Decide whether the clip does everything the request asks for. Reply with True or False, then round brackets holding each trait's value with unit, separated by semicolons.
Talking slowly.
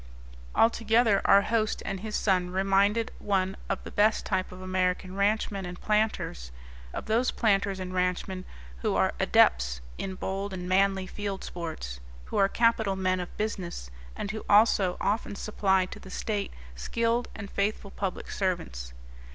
False (155 wpm)